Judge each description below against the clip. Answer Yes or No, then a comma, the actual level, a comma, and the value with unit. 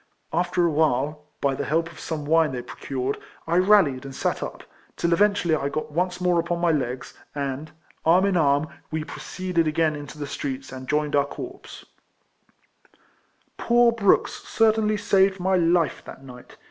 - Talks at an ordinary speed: Yes, average, 170 wpm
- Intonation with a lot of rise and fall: No, average, 4.2 semitones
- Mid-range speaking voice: Yes, medium, 160 Hz